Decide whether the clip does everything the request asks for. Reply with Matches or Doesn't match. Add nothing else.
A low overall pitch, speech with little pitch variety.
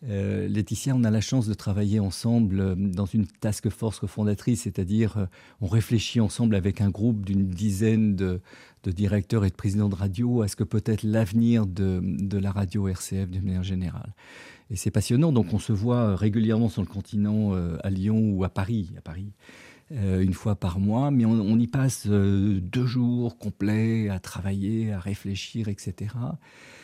Matches